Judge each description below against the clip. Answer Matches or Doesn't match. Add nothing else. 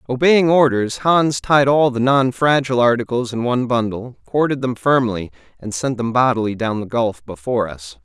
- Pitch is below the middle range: Matches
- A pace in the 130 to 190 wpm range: Matches